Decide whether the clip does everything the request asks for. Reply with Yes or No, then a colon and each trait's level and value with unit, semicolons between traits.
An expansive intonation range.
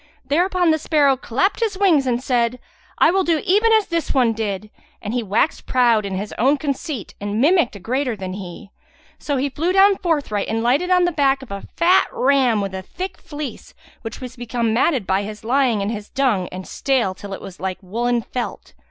Yes: wide, 6.5 semitones